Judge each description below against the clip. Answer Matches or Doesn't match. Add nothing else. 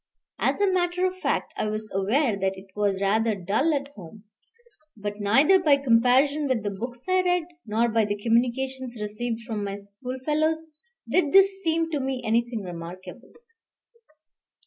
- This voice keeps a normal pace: Matches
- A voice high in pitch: Matches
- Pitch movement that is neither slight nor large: Doesn't match